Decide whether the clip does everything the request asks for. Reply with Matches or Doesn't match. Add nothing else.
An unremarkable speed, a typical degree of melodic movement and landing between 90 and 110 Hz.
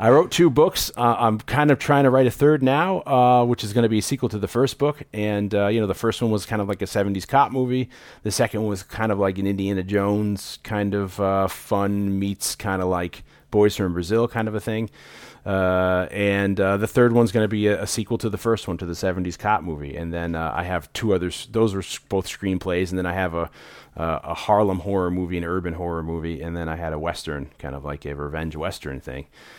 Doesn't match